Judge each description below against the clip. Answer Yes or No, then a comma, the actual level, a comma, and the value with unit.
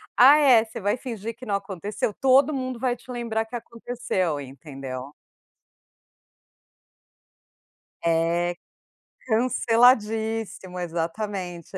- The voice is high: Yes, high, 220 Hz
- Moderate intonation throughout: No, wide, 5.7 semitones